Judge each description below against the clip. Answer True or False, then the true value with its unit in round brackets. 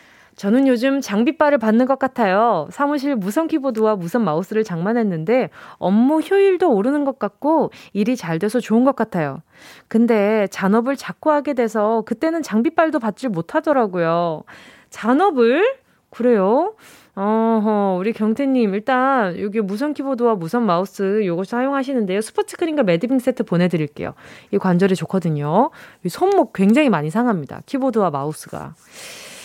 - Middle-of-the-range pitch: False (230 Hz)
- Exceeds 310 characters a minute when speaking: True (330 characters per minute)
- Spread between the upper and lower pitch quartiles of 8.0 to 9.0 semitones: False (5.5 semitones)